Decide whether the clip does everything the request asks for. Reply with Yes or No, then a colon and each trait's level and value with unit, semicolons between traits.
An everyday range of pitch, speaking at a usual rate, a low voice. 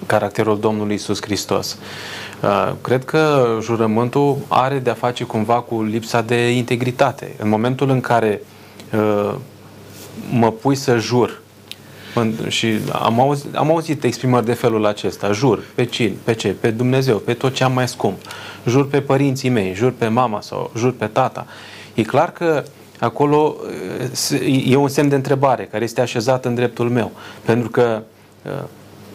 Yes: average, 3.3 semitones; average, 160 wpm; low, 120 Hz